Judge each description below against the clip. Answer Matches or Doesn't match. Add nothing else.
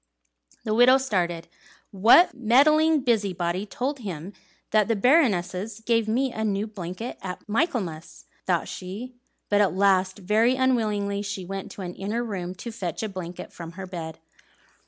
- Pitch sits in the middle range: Doesn't match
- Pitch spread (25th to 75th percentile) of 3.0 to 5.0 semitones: Matches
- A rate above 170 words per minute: Doesn't match